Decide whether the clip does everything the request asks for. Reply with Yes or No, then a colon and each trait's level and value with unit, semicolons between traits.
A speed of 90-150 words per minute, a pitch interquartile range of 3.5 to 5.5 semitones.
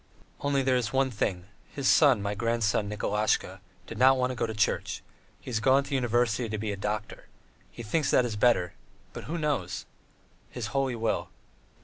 No: average, 200 wpm; average, 3.9 semitones